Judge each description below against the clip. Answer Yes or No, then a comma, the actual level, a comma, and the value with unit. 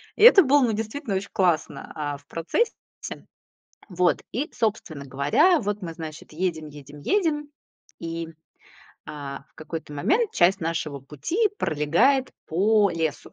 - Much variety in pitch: Yes, wide, 8.3 semitones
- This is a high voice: No, medium, 170 Hz